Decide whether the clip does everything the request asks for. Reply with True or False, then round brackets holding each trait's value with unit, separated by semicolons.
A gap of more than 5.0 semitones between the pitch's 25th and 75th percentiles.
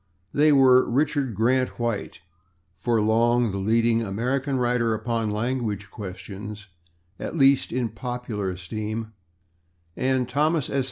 False (3.3 semitones)